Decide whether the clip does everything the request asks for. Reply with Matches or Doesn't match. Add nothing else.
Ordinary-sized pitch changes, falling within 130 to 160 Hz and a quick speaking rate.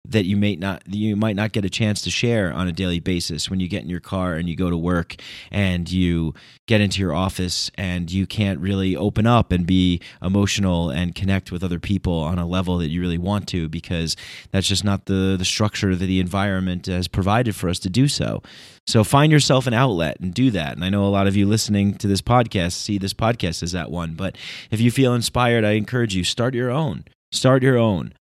Doesn't match